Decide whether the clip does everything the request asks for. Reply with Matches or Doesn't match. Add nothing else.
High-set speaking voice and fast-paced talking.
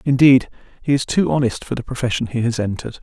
Doesn't match